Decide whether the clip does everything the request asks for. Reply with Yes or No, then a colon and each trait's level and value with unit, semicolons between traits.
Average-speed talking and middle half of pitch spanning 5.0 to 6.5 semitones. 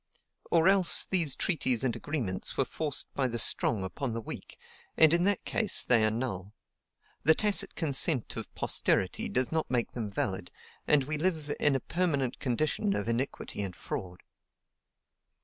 Yes: average, 165 wpm; wide, 5.6 semitones